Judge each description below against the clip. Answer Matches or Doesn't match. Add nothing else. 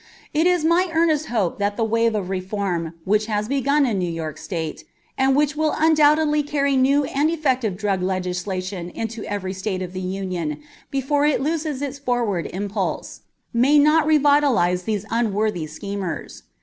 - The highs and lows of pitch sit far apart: Matches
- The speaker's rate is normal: Matches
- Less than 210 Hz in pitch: Doesn't match